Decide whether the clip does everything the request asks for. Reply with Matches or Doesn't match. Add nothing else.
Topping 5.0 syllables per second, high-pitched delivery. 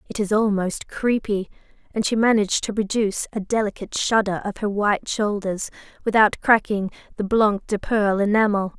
Matches